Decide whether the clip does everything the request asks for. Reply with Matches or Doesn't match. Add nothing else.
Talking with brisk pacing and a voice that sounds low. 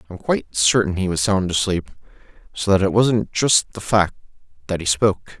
Doesn't match